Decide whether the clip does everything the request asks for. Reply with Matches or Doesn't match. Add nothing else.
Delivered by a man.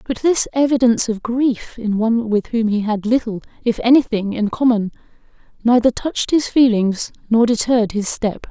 Doesn't match